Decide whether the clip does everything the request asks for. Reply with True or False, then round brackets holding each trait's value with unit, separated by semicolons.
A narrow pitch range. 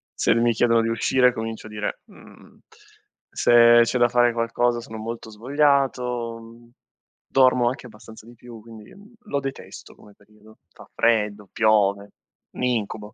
True (1.9 semitones)